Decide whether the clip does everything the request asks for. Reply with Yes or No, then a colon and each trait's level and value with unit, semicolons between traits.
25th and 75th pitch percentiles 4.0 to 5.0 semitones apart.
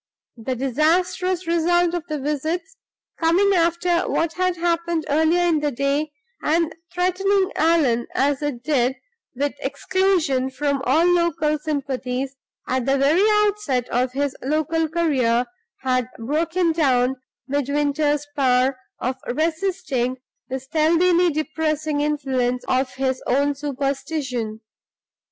Yes: average, 4.3 semitones